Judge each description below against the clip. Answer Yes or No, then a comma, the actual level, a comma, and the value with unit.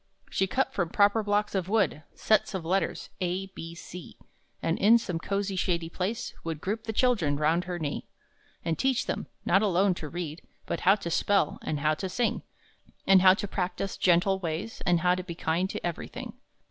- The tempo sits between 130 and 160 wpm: No, average, 195 wpm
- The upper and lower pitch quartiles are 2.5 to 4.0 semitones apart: Yes, average, 3.1 semitones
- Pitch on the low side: No, medium, 185 Hz